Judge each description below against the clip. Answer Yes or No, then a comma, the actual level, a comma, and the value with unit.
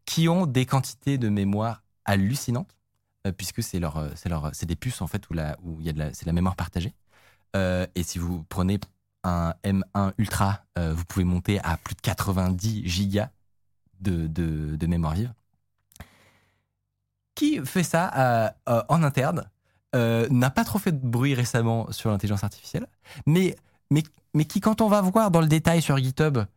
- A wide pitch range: Yes, wide, 5.7 semitones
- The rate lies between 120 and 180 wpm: No, average, 190 wpm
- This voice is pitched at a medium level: No, low, 105 Hz